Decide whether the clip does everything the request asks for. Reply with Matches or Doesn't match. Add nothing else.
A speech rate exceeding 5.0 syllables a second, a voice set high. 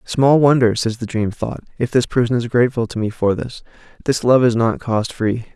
Doesn't match